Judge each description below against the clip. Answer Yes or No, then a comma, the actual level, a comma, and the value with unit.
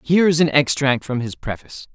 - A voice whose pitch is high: No, low, 135 Hz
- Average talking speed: No, fast, 215 wpm